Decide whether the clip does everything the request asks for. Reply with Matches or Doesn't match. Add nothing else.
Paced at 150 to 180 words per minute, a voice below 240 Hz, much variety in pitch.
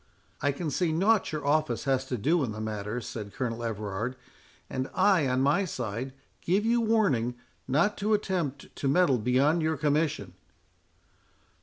Matches